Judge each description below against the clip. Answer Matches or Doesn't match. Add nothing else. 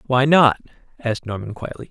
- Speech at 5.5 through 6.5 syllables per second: Matches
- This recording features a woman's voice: Doesn't match